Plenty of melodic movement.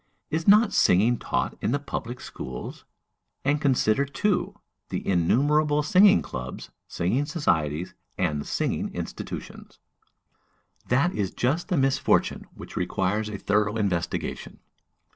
Yes: wide, 7.9 semitones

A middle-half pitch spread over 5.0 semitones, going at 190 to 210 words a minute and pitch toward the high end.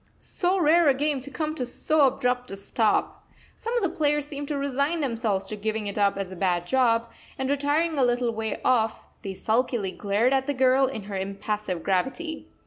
Yes: wide, 5.4 semitones; fast, 205 wpm; very high, 250 Hz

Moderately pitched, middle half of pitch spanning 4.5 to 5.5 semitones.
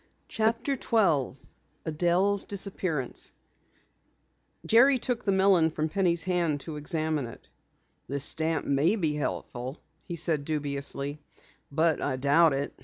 Yes: medium, 160 Hz; average, 4.8 semitones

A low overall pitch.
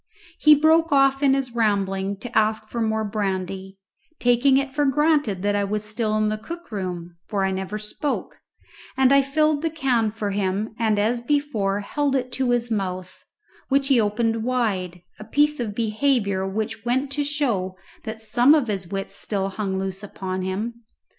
No: high, 220 Hz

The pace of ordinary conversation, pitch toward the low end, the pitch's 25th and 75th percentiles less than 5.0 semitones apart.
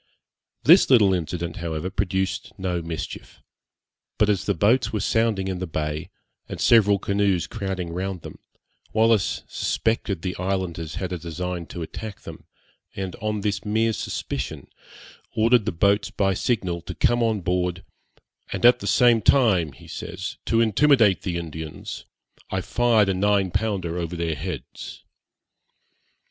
Yes: average, 150 wpm; very low, 95 Hz; average, 3.6 semitones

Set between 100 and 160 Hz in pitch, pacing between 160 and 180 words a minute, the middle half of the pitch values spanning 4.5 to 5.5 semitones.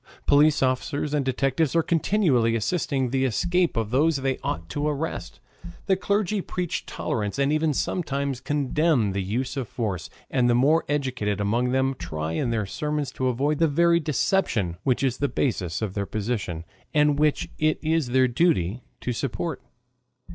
Yes: low, 135 Hz; average, 170 wpm; average, 4.8 semitones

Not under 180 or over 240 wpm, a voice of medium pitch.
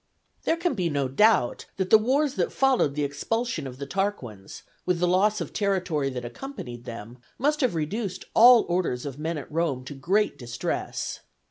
Yes: average, 185 wpm; medium, 175 Hz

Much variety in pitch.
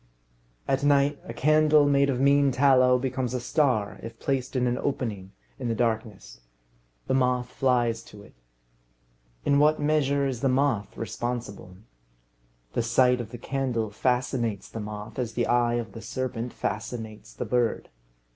No: average, 3.1 semitones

